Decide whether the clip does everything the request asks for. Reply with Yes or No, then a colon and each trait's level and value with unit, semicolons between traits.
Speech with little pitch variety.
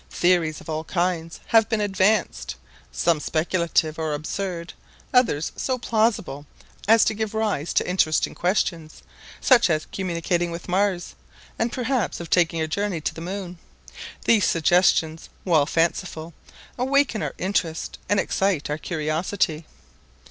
No: average, 4.3 semitones